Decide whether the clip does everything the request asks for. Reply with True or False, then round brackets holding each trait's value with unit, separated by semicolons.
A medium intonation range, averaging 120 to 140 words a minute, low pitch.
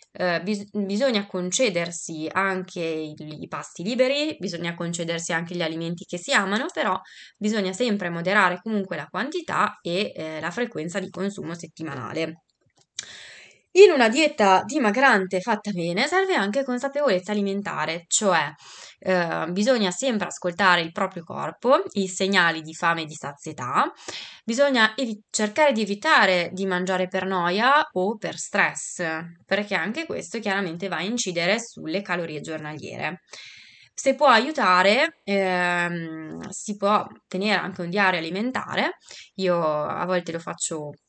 False (3.8 semitones; 135 wpm; 190 Hz)